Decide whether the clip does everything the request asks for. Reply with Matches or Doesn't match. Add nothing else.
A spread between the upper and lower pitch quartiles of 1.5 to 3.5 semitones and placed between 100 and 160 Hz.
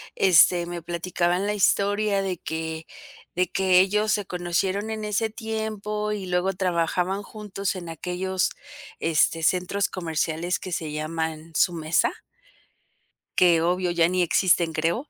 Doesn't match